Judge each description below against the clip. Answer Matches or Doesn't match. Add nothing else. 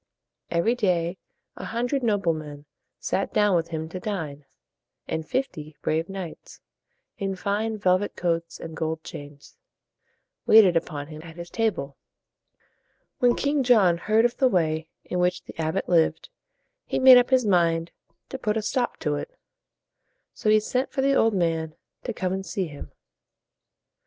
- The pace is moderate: Matches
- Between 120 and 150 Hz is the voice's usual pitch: Doesn't match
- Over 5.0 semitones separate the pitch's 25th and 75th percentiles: Matches